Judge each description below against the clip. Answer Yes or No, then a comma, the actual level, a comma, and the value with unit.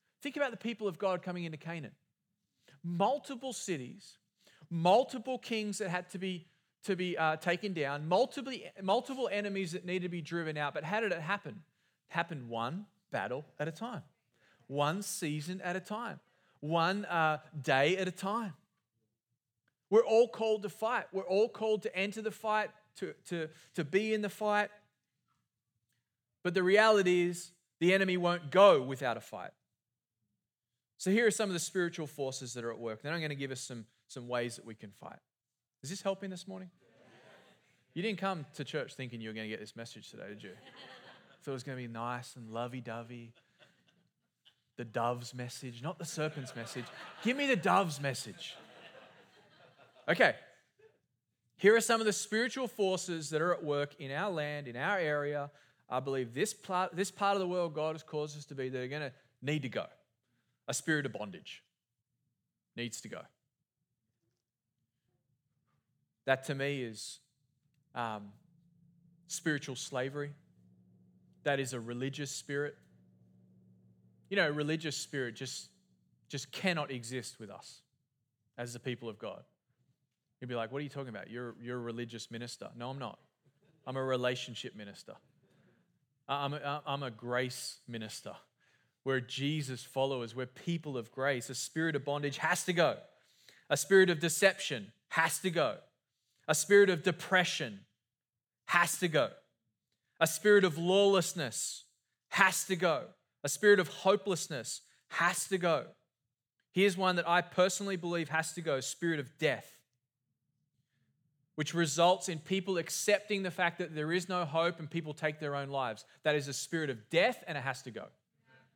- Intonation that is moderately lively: No, wide, 6.4 semitones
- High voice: No, medium, 150 Hz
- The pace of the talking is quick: No, average, 170 wpm